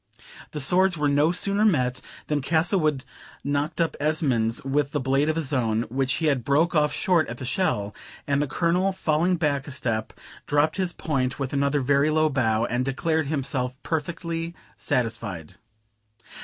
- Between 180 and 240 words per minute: No, average, 170 wpm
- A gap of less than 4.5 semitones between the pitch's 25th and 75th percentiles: Yes, average, 3.8 semitones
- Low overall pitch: No, medium, 145 Hz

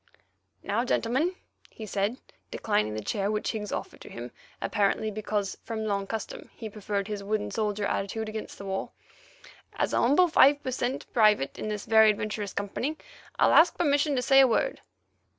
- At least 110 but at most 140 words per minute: No, average, 175 wpm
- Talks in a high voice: Yes, high, 215 Hz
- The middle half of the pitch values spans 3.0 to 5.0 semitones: Yes, average, 3.5 semitones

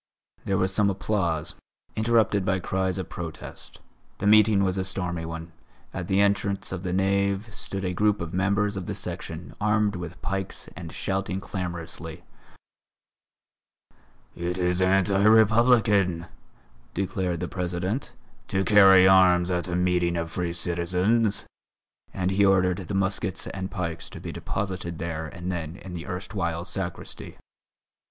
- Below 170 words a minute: Yes, average, 145 wpm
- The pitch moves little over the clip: Yes, narrow, 2.1 semitones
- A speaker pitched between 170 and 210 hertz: No, very low, 95 Hz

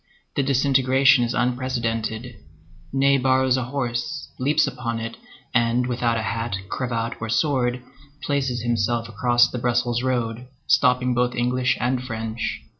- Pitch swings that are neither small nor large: No, narrow, 1.8 semitones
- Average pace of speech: No, slow, 130 wpm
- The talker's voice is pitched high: No, low, 125 Hz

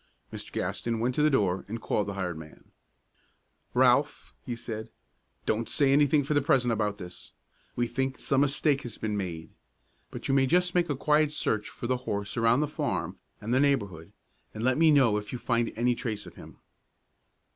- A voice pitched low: Yes, low, 120 Hz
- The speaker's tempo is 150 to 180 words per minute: No, average, 195 wpm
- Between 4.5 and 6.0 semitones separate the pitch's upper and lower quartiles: Yes, average, 4.8 semitones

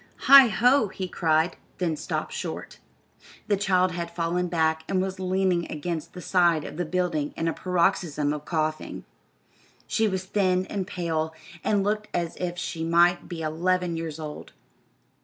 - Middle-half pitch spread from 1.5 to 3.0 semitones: Yes, narrow, 2.5 semitones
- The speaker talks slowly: No, average, 160 wpm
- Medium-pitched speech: Yes, medium, 175 Hz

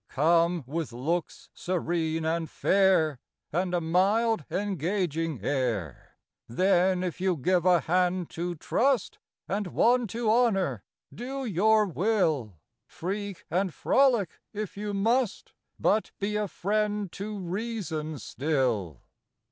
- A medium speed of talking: No, slow, 120 wpm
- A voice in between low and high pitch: Yes, medium, 180 Hz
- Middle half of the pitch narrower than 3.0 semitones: No, average, 4.6 semitones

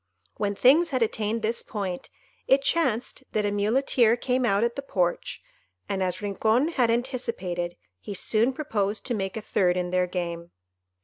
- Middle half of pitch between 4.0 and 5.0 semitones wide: Yes, average, 4.5 semitones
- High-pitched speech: Yes, high, 215 Hz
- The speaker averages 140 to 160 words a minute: No, average, 170 wpm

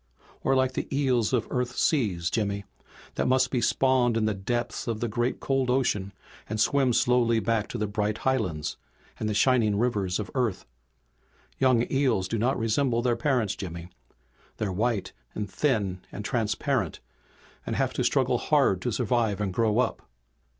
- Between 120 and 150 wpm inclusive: No, average, 170 wpm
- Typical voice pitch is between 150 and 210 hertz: No, low, 115 Hz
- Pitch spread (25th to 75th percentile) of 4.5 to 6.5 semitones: No, average, 3.4 semitones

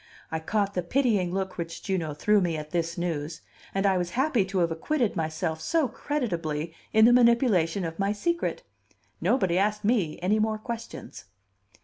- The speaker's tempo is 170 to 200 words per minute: Yes, average, 175 wpm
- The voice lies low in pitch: No, high, 190 Hz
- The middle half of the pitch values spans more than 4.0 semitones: Yes, average, 5.0 semitones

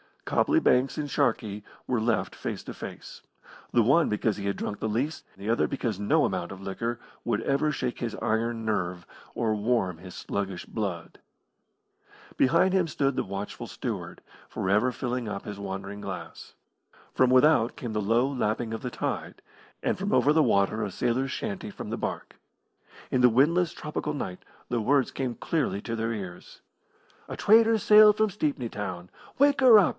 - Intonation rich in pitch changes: Yes, wide, 5.7 semitones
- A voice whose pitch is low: Yes, low, 115 Hz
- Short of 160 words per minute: No, average, 180 wpm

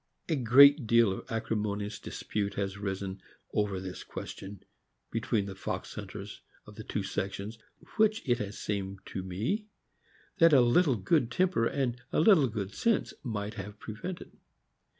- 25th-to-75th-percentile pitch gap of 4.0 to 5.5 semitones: Yes, average, 5.2 semitones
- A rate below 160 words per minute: Yes, average, 150 wpm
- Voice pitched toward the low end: Yes, low, 110 Hz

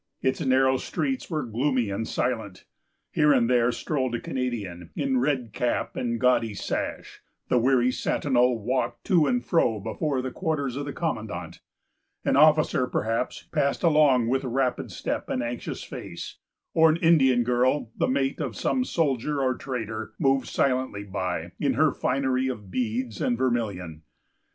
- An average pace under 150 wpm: No, average, 155 wpm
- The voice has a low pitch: Yes, low, 130 Hz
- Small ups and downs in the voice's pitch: No, average, 3.3 semitones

